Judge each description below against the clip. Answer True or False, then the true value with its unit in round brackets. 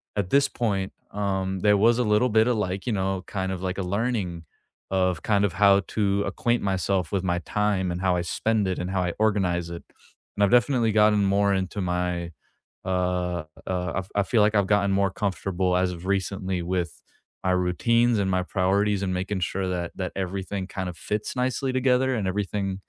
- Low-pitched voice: True (95 Hz)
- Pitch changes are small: True (2.3 semitones)